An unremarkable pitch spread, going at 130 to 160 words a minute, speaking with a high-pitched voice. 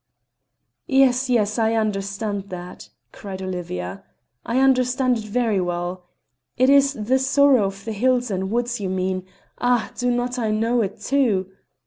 Yes: average, 4.7 semitones; average, 150 wpm; high, 220 Hz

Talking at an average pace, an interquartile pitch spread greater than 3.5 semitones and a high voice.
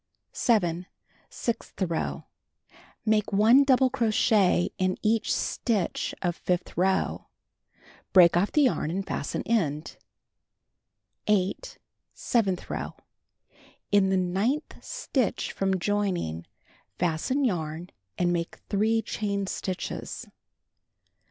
No: slow, 100 wpm; average, 4.0 semitones; high, 195 Hz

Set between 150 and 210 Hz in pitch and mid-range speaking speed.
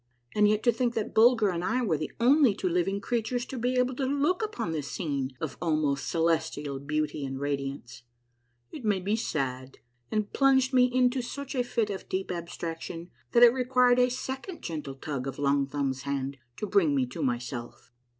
Yes: medium, 185 Hz; average, 190 wpm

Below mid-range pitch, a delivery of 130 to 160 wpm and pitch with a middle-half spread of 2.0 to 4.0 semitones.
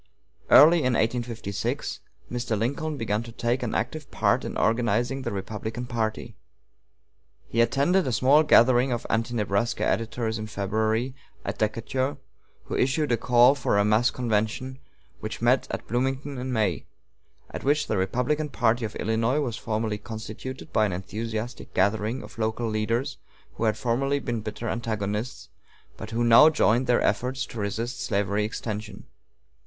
Yes: low, 115 Hz; average, 155 wpm; average, 2.8 semitones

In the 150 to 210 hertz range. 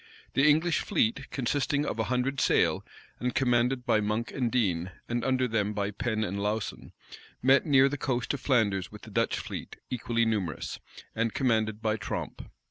No: low, 120 Hz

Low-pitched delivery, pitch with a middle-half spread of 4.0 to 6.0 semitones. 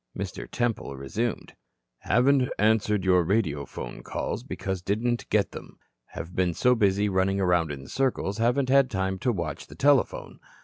Yes: low, 100 Hz; average, 5.2 semitones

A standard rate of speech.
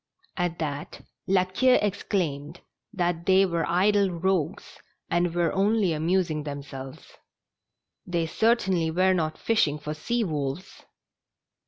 No: slow, 125 wpm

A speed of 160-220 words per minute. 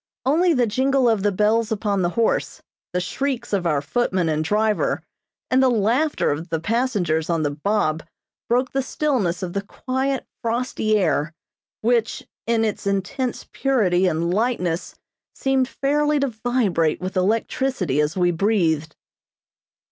No: average, 150 wpm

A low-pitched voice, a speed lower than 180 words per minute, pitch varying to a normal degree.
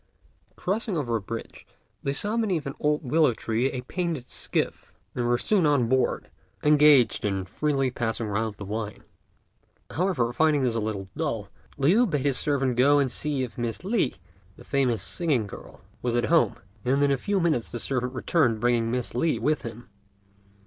No: low, 130 Hz; average, 185 wpm; average, 4.4 semitones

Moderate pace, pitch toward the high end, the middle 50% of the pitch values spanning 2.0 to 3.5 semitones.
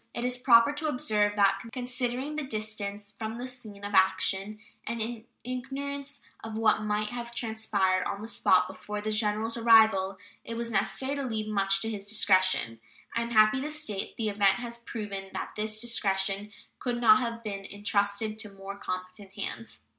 Yes: average, 180 wpm; high, 215 Hz; average, 2.9 semitones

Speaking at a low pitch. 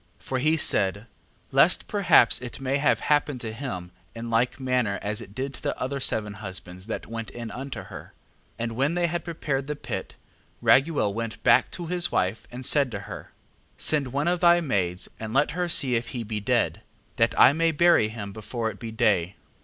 Yes: low, 125 Hz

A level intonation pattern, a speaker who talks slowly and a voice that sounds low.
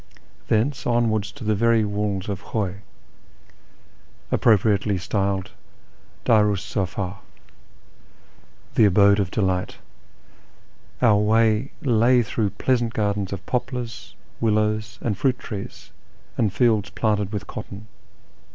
Yes: narrow, 2.2 semitones; slow, 115 wpm; low, 105 Hz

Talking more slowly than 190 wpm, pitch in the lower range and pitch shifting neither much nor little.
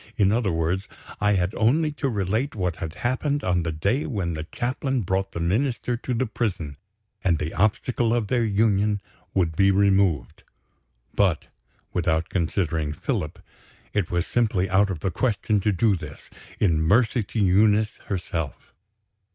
Yes: average, 160 wpm; low, 100 Hz; average, 4.7 semitones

